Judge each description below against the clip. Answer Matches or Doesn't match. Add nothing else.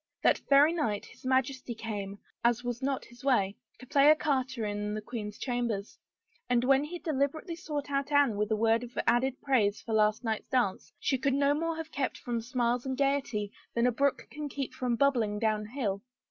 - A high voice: Matches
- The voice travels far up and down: Doesn't match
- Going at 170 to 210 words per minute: Matches